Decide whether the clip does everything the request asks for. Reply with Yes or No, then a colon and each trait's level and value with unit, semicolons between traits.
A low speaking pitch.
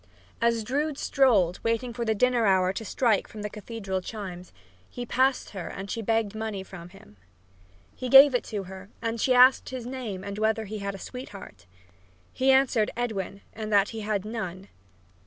No: high, 220 Hz